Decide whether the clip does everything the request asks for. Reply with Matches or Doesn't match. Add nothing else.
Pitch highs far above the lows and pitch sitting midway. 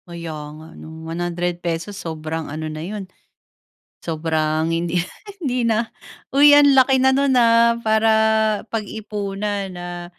Matches